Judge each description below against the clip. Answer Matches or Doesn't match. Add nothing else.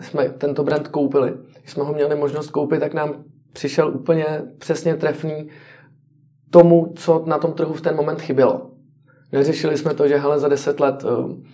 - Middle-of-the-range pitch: Matches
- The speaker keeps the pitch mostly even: Matches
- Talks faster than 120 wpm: Matches